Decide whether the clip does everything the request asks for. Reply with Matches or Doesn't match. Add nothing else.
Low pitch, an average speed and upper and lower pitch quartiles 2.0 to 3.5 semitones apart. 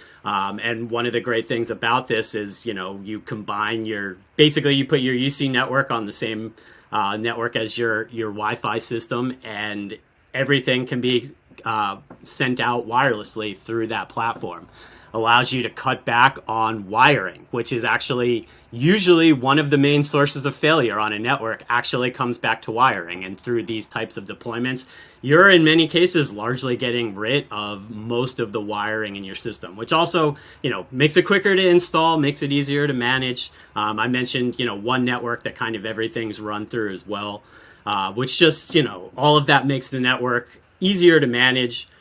Doesn't match